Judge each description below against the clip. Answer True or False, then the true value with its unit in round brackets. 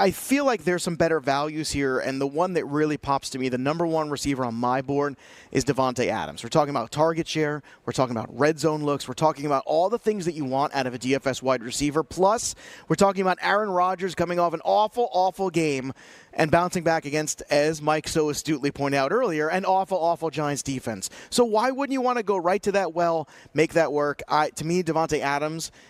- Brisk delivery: True (230 wpm)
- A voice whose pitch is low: False (155 Hz)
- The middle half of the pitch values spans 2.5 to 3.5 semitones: False (4.1 semitones)